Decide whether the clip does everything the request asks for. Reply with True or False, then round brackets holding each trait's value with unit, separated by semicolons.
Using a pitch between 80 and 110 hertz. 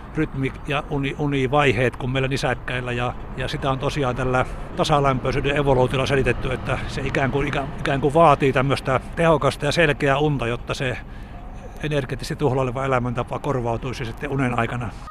False (135 Hz)